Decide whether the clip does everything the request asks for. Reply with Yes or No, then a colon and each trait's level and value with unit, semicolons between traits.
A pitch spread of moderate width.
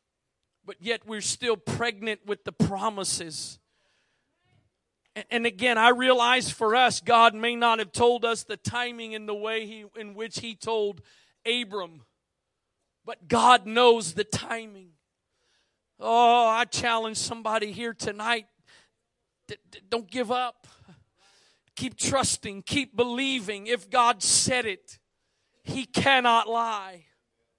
No: narrow, 2.2 semitones